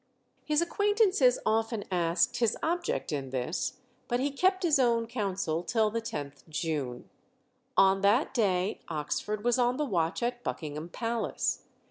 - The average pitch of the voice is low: No, high, 220 Hz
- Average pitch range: No, wide, 6.8 semitones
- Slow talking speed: No, average, 145 wpm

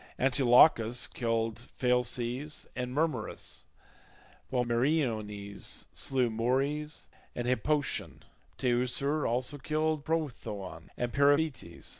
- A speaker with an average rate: No, slow, 85 wpm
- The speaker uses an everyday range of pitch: Yes, average, 3.7 semitones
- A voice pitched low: Yes, low, 125 Hz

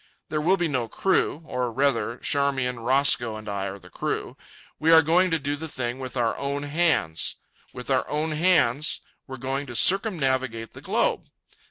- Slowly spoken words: No, average, 180 wpm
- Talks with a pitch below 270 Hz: Yes, medium, 140 Hz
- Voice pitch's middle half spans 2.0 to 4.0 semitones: No, average, 4.6 semitones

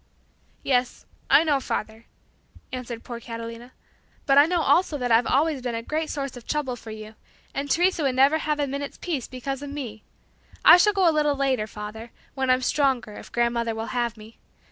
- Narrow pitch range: No, average, 3.8 semitones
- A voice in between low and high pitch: No, very high, 260 Hz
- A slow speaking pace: No, average, 195 wpm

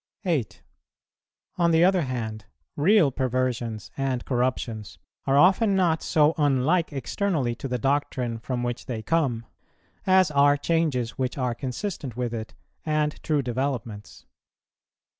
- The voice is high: No, low, 135 Hz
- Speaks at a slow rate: Yes, slow, 130 wpm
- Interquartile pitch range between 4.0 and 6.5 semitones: Yes, average, 4.7 semitones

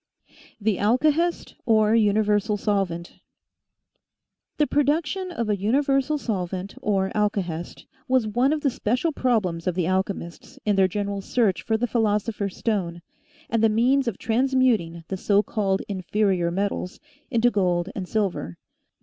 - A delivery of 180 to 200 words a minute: No, average, 140 wpm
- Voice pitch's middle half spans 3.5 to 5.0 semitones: Yes, average, 4.2 semitones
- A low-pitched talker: No, high, 210 Hz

